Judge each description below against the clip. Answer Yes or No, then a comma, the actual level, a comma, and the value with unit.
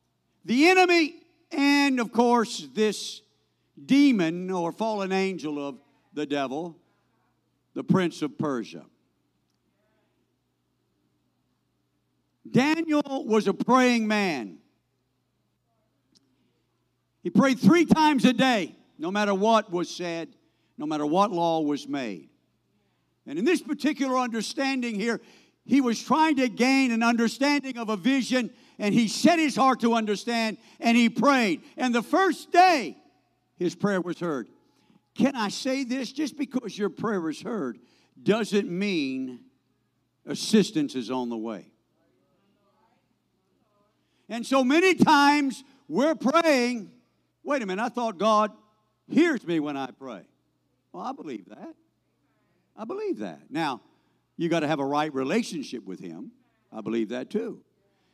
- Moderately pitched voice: No, high, 225 Hz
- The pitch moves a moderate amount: No, wide, 8.0 semitones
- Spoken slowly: Yes, slow, 130 wpm